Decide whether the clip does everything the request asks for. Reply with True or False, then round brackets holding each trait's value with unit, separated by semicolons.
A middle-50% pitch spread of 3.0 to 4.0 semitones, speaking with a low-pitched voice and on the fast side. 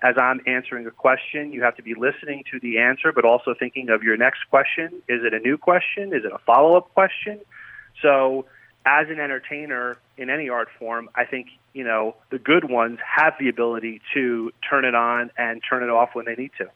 True (3.5 semitones; 125 Hz; 220 wpm)